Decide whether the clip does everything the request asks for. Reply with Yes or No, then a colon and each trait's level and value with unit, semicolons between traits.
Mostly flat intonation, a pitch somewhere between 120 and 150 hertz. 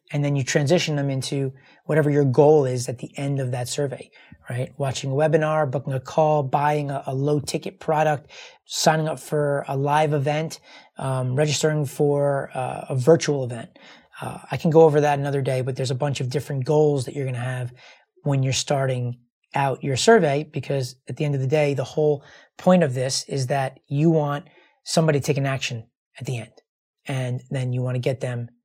Yes: narrow, 2.3 semitones; medium, 140 Hz